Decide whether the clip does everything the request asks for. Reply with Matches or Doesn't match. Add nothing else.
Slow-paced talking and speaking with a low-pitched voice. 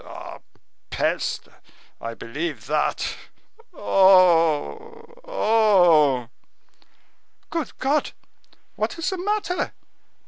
Doesn't match